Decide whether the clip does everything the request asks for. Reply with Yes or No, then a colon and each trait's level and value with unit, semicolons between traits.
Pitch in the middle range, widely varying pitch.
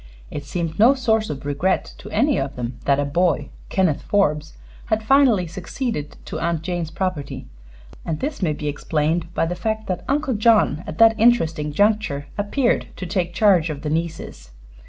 Yes: medium, 175 Hz; wide, 6.3 semitones